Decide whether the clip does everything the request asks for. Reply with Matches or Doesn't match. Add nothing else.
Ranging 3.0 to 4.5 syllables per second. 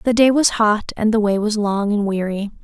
Doesn't match